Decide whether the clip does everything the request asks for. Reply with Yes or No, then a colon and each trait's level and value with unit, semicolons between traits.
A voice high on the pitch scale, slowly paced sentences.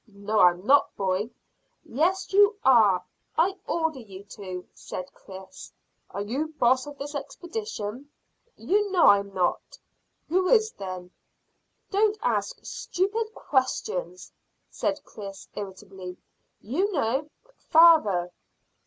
Yes: very high, 260 Hz; slow, 115 wpm